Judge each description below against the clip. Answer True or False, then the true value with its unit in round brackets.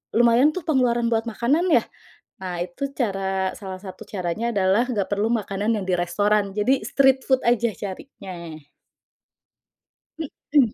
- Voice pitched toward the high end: True (210 Hz)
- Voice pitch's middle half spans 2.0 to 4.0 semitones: False (4.4 semitones)